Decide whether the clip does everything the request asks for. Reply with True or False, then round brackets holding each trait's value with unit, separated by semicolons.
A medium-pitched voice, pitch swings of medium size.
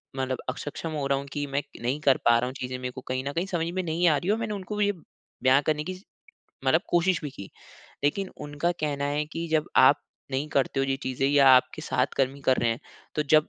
True (145 Hz; 3.6 semitones)